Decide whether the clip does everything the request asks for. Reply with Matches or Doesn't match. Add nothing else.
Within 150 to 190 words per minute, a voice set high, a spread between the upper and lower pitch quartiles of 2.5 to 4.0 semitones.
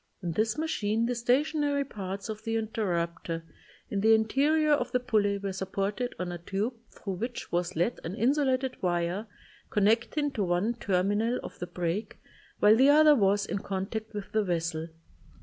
Doesn't match